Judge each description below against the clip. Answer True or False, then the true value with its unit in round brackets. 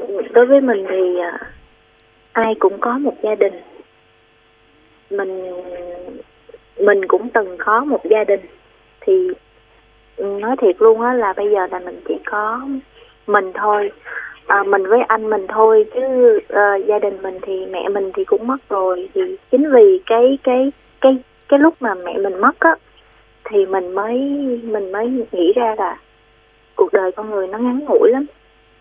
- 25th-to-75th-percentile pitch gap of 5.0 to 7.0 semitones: True (5.6 semitones)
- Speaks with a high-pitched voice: True (220 Hz)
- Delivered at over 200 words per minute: False (165 wpm)